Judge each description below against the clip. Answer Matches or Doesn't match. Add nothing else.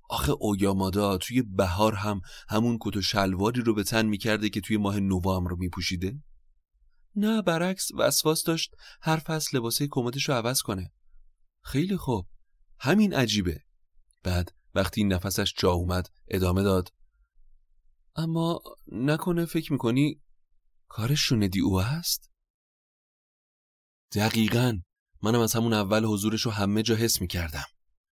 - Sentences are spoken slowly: Doesn't match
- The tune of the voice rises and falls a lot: Matches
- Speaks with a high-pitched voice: Doesn't match